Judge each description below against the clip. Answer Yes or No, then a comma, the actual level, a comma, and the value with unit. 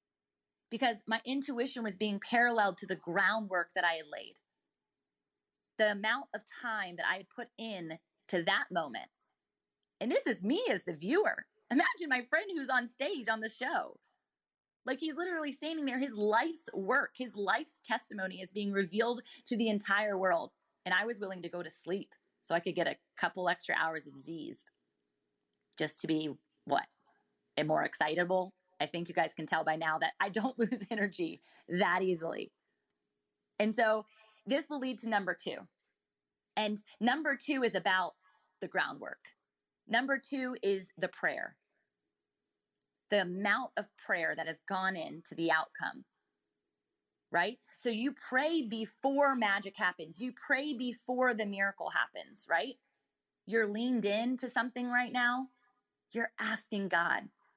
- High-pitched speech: Yes, high, 215 Hz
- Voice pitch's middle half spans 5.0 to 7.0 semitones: Yes, wide, 5.4 semitones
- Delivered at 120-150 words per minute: No, average, 160 wpm